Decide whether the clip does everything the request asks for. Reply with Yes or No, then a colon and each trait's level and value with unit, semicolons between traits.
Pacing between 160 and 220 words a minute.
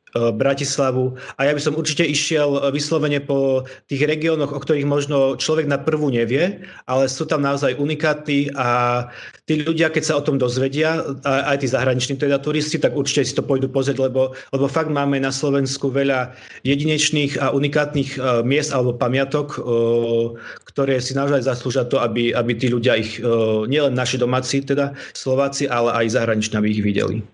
Yes: fast, 165 wpm